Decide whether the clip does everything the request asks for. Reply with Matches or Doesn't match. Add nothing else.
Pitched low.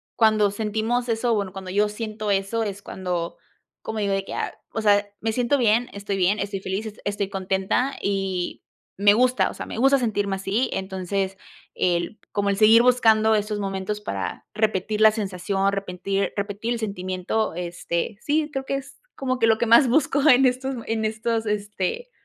Doesn't match